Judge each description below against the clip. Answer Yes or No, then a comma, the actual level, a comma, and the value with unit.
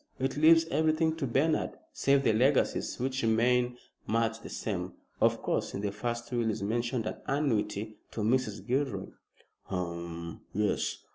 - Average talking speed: Yes, average, 150 wpm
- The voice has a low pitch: Yes, low, 120 Hz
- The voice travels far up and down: No, average, 4.1 semitones